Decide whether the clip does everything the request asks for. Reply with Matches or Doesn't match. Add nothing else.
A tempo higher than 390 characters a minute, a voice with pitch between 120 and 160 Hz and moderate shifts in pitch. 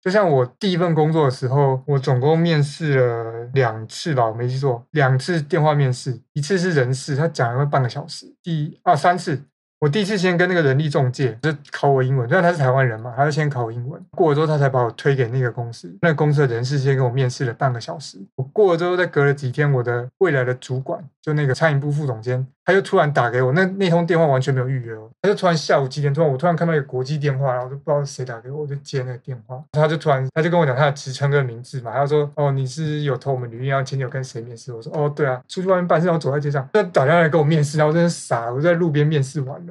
Matches